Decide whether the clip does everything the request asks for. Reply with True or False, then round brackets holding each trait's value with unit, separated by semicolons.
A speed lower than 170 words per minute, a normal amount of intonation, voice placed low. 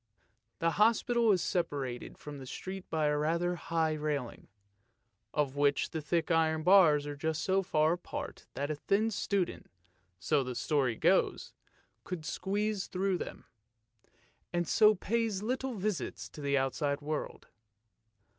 False (150 wpm; 4.9 semitones; 160 Hz)